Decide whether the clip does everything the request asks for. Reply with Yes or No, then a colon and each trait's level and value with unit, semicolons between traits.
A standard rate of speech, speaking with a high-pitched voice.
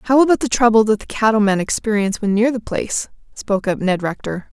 No: fast, 220 wpm; high, 220 Hz